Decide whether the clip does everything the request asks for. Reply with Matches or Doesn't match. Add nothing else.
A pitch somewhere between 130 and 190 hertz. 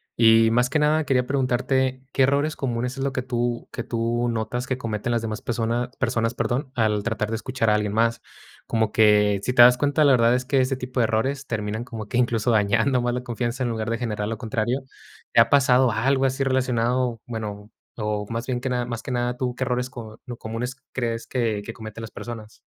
Doesn't match